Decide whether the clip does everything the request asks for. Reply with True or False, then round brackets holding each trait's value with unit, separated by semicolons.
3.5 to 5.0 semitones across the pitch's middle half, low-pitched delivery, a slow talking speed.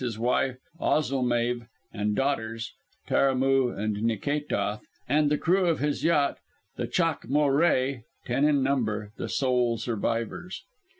True (3.9 semitones; 130 Hz; 130 wpm)